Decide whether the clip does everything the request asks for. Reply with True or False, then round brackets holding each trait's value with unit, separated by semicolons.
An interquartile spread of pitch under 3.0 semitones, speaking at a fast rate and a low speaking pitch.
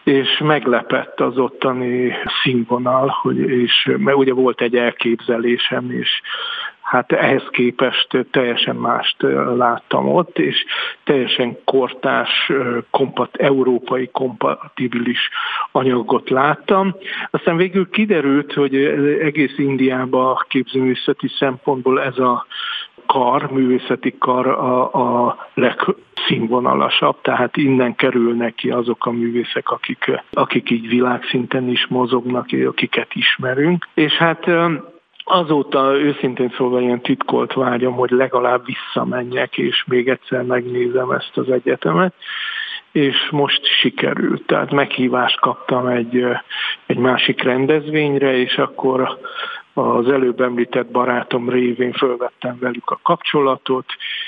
False (2.4 semitones; 110 wpm; 130 Hz)